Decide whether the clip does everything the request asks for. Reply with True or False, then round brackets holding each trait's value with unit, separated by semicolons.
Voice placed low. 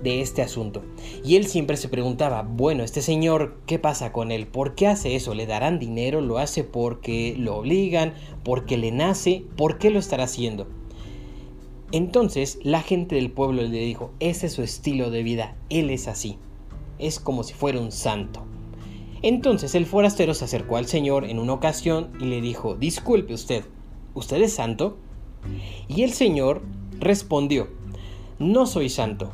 True (130 Hz)